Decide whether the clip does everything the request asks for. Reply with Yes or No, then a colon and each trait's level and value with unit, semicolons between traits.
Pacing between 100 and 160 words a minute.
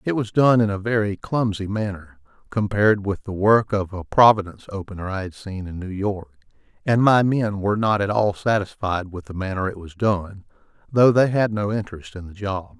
No: fast, 205 wpm